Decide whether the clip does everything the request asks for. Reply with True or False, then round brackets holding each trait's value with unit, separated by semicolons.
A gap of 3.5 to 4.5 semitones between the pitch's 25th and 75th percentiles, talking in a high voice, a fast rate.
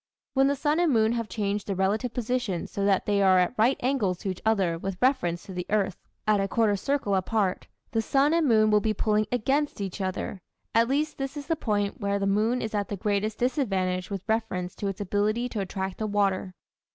True (3.8 semitones; 210 Hz; 225 wpm)